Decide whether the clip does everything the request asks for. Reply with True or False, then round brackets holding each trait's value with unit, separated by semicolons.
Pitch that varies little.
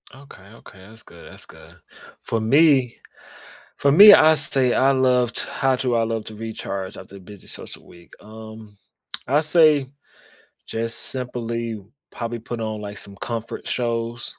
False (3.2 semitones)